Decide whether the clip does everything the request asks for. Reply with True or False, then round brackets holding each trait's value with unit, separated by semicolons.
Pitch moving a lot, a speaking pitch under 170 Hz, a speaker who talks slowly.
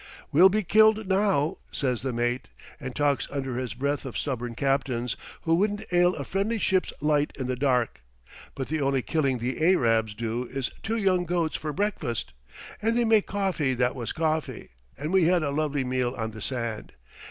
False (6.3 semitones; 140 Hz; 185 wpm)